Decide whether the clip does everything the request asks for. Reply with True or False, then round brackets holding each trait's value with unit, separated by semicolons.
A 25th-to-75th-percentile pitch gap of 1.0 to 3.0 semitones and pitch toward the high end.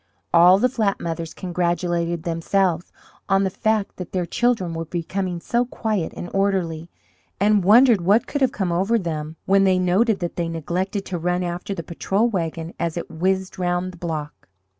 False (2.6 semitones; 180 Hz)